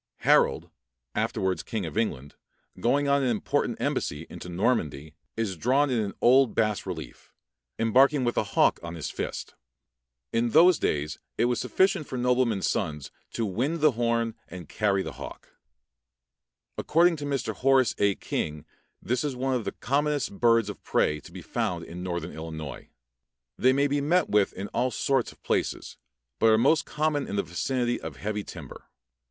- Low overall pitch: Yes, low, 115 Hz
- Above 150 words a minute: Yes, average, 170 wpm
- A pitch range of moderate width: No, wide, 6.3 semitones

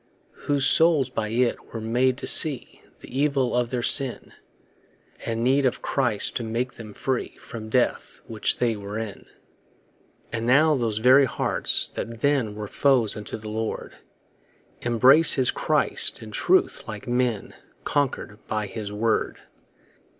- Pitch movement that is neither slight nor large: Yes, average, 3.2 semitones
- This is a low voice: Yes, low, 120 Hz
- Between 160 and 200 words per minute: No, average, 150 wpm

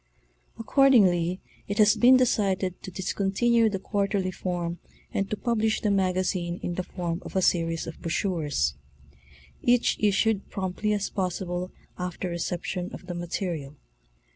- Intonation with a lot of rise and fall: No, average, 2.9 semitones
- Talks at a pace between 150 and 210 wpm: No, average, 140 wpm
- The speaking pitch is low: No, medium, 185 Hz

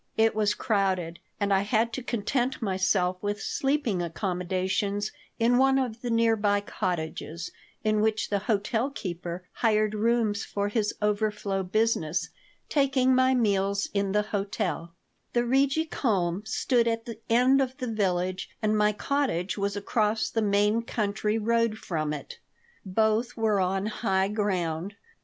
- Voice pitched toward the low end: No, high, 210 Hz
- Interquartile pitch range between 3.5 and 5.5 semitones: No, average, 3.1 semitones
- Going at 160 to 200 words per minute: No, average, 145 wpm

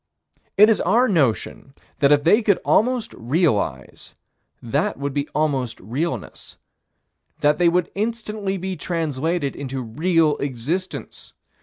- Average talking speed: No, slow, 125 wpm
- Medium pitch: Yes, medium, 155 Hz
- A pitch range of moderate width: No, wide, 5.8 semitones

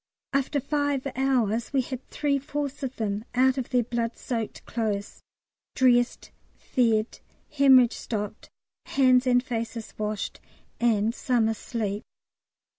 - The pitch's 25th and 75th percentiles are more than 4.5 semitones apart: No, average, 3.0 semitones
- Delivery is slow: Yes, slow, 120 wpm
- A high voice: Yes, high, 245 Hz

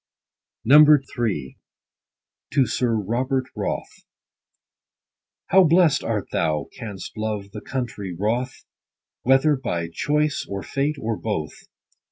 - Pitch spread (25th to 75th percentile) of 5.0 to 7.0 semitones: Yes, average, 5.3 semitones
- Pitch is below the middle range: Yes, low, 120 Hz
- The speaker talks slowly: Yes, slow, 110 wpm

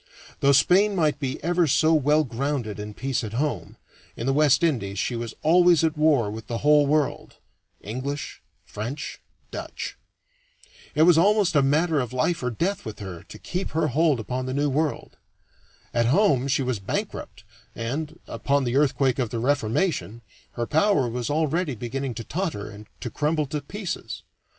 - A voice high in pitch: No, medium, 140 Hz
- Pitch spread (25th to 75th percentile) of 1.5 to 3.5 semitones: No, average, 4.8 semitones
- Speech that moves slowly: No, average, 175 wpm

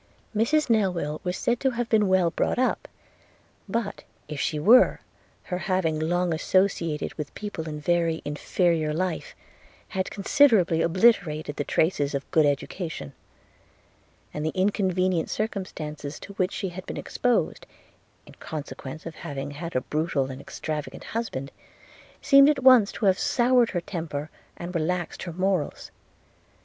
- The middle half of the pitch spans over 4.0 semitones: Yes, average, 4.7 semitones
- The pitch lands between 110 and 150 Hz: No, medium, 175 Hz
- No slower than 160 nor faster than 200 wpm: No, average, 145 wpm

